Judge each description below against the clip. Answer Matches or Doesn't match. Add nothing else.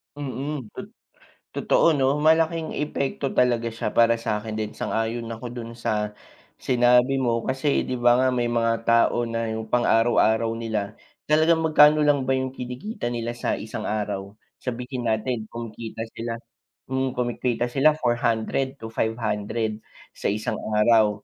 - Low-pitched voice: Matches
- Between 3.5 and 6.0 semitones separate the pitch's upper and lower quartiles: Doesn't match